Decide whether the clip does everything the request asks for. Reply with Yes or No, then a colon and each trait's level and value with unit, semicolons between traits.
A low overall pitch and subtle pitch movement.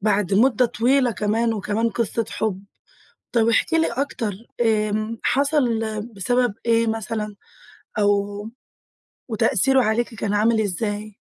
No: high, 220 Hz; narrow, 2.2 semitones